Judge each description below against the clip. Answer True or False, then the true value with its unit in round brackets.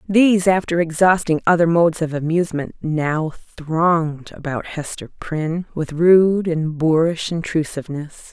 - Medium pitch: True (165 Hz)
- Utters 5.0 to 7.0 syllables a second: False (4.6 syllables/s)